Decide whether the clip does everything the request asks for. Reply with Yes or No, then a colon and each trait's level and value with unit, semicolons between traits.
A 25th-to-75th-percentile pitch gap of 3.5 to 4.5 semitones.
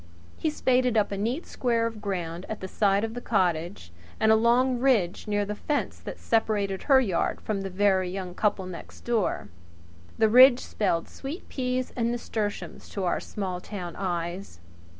Yes: average, 4.2 semitones